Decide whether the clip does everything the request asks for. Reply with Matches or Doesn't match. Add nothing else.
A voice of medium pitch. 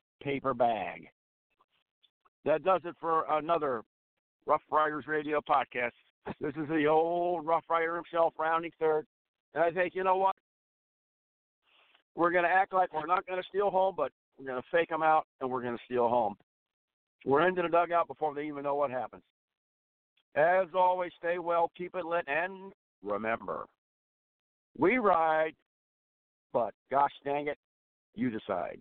Matches